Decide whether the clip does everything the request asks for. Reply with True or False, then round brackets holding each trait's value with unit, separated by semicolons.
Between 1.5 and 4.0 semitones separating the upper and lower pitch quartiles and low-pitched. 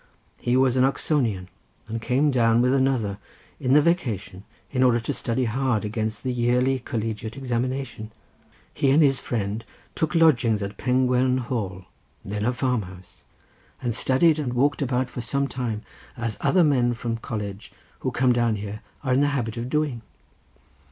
True (2.9 semitones; 125 Hz)